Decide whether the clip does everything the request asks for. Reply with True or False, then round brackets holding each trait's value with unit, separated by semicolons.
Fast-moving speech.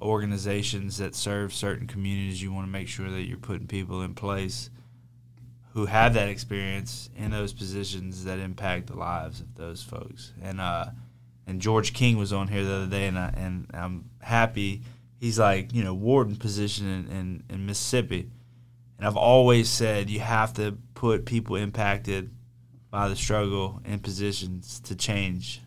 False (170 wpm)